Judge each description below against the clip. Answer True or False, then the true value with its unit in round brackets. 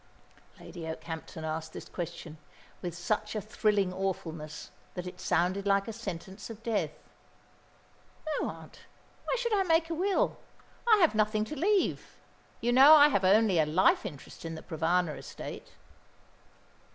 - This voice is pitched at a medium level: False (195 Hz)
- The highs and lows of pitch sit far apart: True (6.2 semitones)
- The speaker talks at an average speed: True (150 wpm)